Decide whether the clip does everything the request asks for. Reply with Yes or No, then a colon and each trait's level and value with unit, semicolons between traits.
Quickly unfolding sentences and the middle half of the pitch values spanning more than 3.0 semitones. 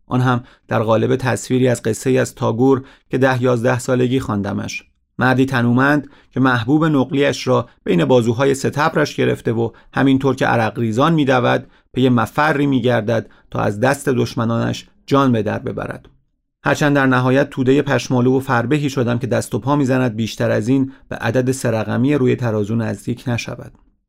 No: fast, 165 wpm; narrow, 2.6 semitones